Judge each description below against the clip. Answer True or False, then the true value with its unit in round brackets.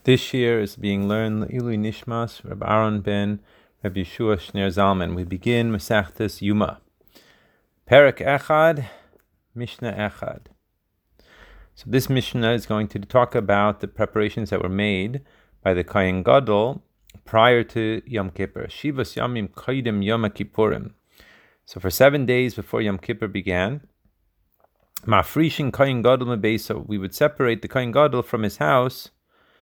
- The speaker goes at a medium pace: True (140 wpm)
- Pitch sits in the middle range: False (110 Hz)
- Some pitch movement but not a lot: True (3.5 semitones)